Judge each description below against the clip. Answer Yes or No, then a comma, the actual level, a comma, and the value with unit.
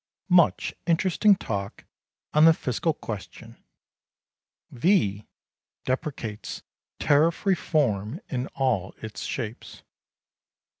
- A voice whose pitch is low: Yes, low, 130 Hz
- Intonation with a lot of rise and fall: Yes, wide, 7.3 semitones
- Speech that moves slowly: Yes, slow, 85 wpm